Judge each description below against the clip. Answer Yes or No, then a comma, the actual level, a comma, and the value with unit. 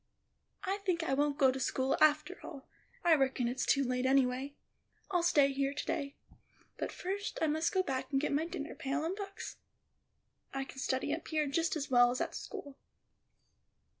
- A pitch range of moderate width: Yes, average, 3.5 semitones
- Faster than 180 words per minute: Yes, average, 190 wpm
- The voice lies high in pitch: Yes, very high, 285 Hz